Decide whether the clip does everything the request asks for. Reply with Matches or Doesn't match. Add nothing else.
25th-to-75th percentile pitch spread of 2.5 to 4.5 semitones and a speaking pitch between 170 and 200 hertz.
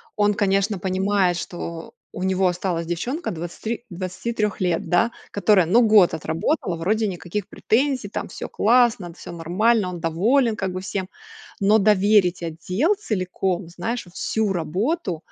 Matches